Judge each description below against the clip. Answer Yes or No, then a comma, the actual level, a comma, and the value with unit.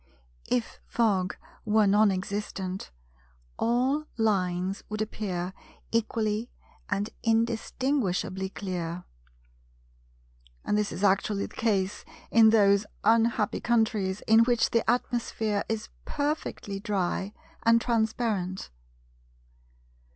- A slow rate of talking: Yes, slow, 95 wpm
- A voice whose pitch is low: No, high, 210 Hz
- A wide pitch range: No, average, 3.0 semitones